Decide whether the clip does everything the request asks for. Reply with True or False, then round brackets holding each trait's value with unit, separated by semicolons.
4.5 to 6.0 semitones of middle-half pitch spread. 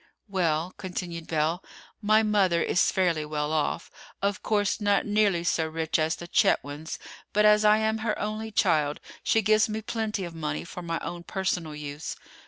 True (4.8 semitones)